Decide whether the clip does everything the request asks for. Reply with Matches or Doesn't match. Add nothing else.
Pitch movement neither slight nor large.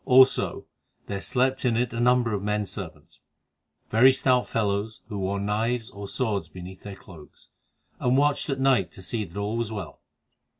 Matches